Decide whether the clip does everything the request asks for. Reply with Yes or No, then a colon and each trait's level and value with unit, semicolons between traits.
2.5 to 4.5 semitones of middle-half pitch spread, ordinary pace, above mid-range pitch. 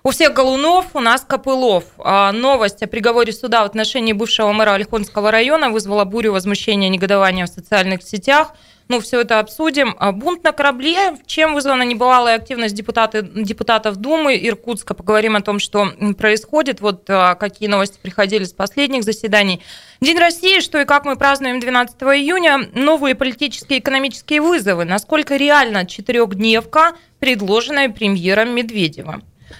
No: average, 5.0 semitones; average, 150 wpm; high, 230 Hz